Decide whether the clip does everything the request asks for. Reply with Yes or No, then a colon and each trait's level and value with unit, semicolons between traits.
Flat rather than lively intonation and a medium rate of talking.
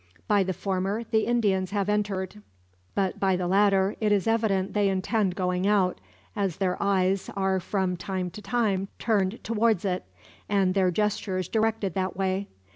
Yes: narrow, 1.9 semitones; average, 165 wpm